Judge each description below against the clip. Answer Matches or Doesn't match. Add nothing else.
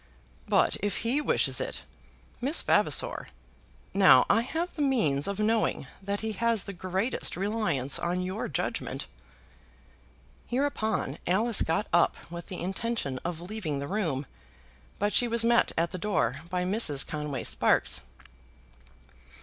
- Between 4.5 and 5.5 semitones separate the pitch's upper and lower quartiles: Matches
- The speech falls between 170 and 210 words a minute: Doesn't match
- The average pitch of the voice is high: Matches